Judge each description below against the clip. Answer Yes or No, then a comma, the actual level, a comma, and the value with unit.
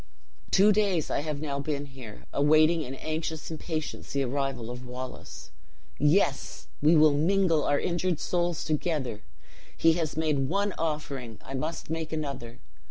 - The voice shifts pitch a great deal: No, average, 3.0 semitones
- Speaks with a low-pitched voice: No, medium, 155 Hz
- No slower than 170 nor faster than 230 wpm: No, average, 150 wpm